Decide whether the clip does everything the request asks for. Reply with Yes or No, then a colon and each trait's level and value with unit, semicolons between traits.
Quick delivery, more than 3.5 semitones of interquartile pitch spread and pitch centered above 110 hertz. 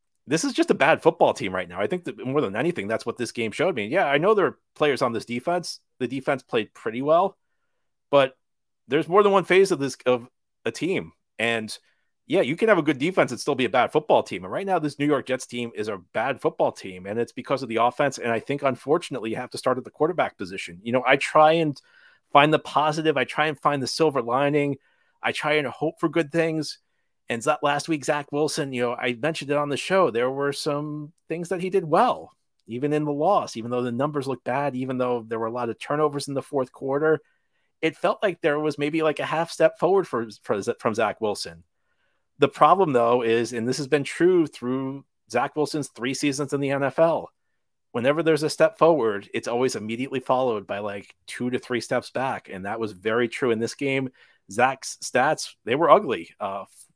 Yes: fast, 225 wpm; average, 4.0 semitones; medium, 140 Hz